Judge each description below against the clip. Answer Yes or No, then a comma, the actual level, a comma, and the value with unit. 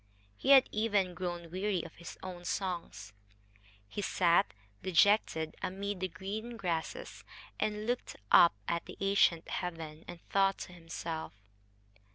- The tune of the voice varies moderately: Yes, average, 3.2 semitones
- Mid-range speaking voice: Yes, medium, 180 Hz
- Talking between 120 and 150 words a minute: Yes, slow, 135 wpm